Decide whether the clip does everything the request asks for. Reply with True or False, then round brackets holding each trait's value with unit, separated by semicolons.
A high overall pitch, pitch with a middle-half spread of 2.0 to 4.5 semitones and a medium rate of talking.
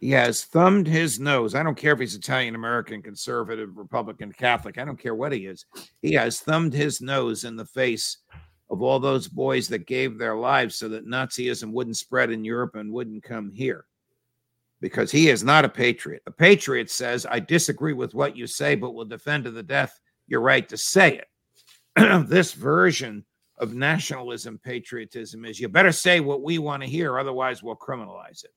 False (125 Hz; 4.2 semitones; 195 wpm)